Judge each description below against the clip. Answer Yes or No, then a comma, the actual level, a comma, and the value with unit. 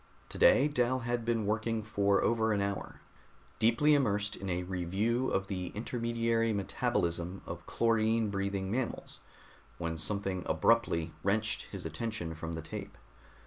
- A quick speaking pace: No, average, 140 wpm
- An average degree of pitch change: Yes, average, 3.6 semitones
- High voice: No, low, 105 Hz